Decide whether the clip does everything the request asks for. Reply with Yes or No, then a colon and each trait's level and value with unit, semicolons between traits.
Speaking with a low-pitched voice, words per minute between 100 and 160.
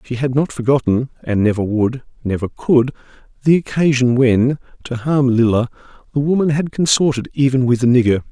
Yes: low, 130 Hz; average, 145 wpm